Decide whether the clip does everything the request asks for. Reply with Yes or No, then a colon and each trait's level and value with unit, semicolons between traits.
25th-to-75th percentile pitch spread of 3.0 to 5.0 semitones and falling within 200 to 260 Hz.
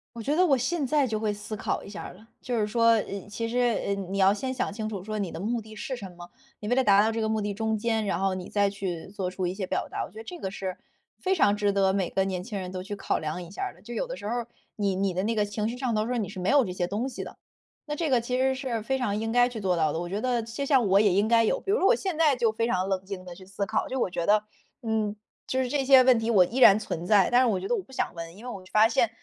Yes: average, 4.0 semitones; high, 215 Hz